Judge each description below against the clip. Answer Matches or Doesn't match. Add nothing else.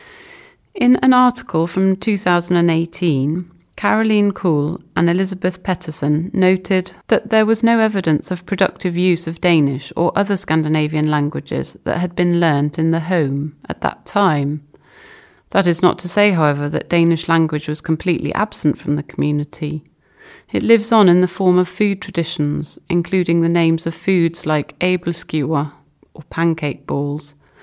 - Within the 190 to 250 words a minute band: Doesn't match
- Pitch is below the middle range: Doesn't match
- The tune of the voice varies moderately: Matches